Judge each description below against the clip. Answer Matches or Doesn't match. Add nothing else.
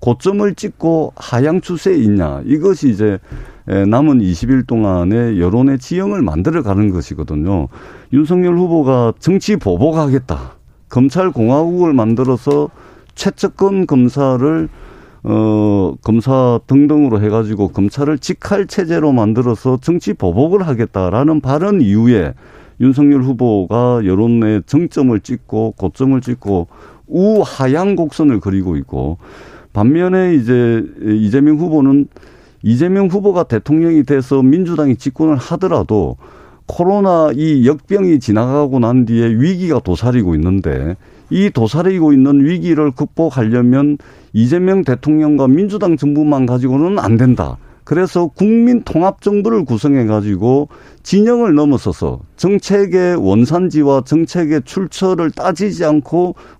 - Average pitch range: Doesn't match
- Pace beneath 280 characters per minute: Doesn't match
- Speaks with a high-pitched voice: Doesn't match